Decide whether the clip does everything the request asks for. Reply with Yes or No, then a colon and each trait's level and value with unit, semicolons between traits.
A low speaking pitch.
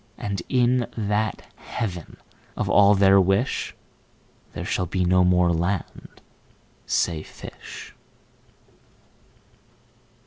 Yes: very low, 95 Hz